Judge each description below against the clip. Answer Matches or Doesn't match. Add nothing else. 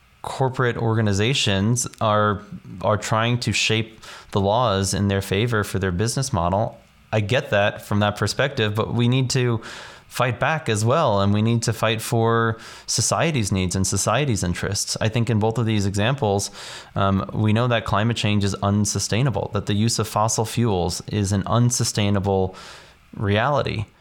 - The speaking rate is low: Doesn't match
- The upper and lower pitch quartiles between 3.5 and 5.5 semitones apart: Doesn't match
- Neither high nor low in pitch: Doesn't match